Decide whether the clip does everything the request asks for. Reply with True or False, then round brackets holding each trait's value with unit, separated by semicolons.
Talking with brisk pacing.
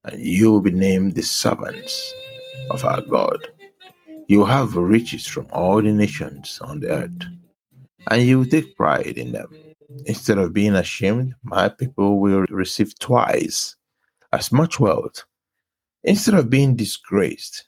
False (145 wpm)